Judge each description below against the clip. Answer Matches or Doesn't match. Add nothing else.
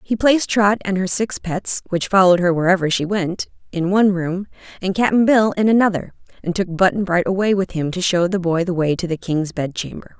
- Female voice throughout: Matches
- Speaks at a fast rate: Matches